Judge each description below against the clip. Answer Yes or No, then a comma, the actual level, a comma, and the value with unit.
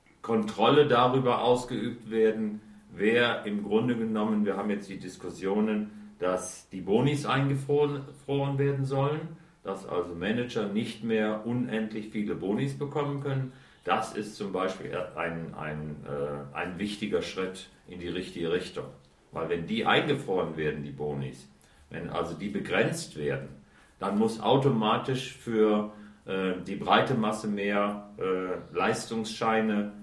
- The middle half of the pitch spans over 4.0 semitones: Yes, average, 5.2 semitones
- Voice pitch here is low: Yes, low, 105 Hz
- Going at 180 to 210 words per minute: No, average, 135 wpm